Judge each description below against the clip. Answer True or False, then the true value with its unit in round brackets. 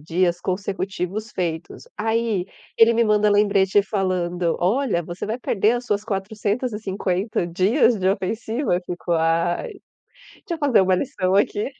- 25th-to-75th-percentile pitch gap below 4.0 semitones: True (3.5 semitones)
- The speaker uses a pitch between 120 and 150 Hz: False (195 Hz)